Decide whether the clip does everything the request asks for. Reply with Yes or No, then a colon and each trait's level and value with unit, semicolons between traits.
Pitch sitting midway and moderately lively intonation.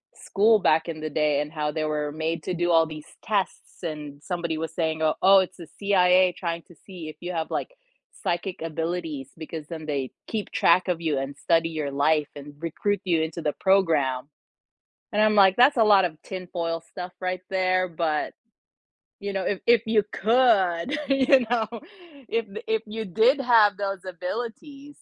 Yes: medium, 175 Hz; average, 4.1 semitones